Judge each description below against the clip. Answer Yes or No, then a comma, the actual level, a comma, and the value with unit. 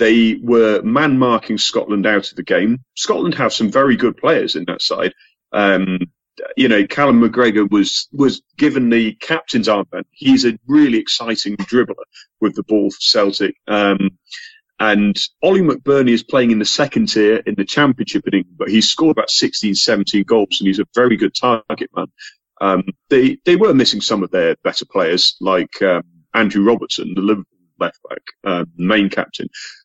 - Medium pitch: No, low, 110 Hz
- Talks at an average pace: Yes, average, 175 wpm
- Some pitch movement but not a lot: Yes, average, 4.0 semitones